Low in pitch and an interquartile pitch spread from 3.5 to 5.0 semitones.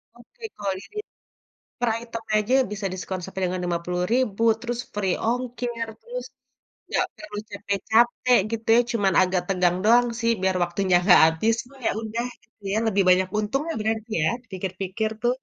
No: high, 215 Hz; average, 4.0 semitones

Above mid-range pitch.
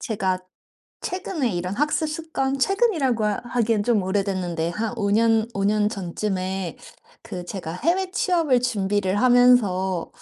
Yes: high, 215 Hz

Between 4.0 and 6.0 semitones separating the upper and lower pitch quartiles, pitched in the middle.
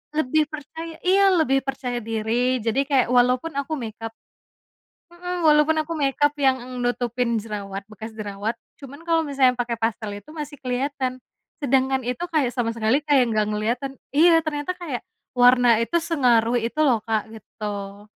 No: average, 4.5 semitones; very high, 255 Hz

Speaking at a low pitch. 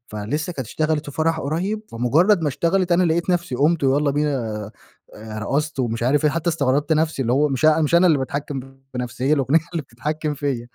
No: medium, 145 Hz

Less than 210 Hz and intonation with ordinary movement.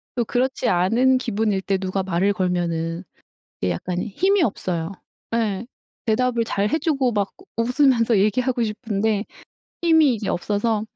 No: high, 215 Hz; average, 4.5 semitones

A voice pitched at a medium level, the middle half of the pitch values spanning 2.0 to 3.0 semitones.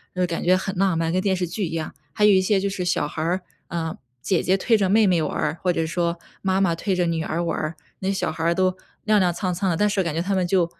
Yes: medium, 180 Hz; narrow, 2.4 semitones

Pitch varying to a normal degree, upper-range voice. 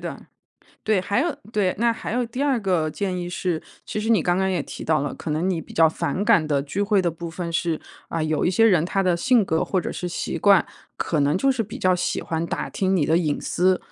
No: average, 3.8 semitones; medium, 180 Hz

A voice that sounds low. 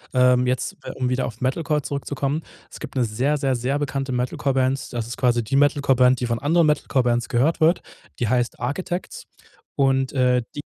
Yes: low, 130 Hz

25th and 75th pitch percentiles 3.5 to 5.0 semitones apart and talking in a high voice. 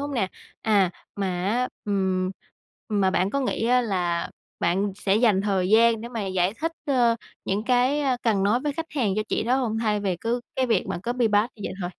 Yes: average, 4.3 semitones; high, 215 Hz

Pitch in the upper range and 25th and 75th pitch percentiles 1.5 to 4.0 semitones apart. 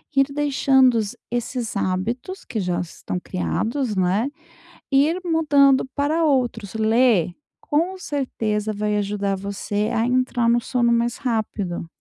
No: high, 235 Hz; average, 4.8 semitones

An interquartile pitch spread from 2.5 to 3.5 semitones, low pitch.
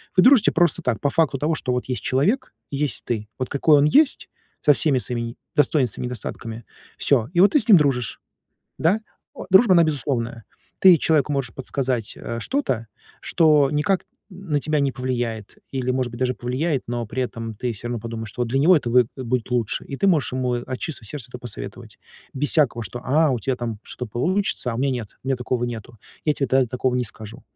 No: average, 3.9 semitones; low, 130 Hz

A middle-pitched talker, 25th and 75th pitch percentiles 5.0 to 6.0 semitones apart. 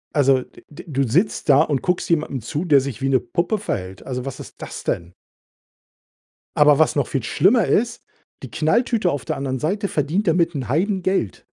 Yes: medium, 150 Hz; wide, 5.5 semitones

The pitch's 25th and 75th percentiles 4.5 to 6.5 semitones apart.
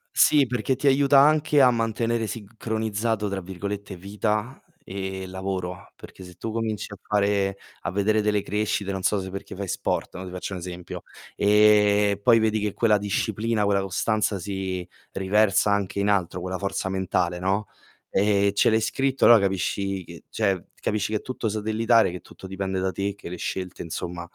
No: narrow, 2.4 semitones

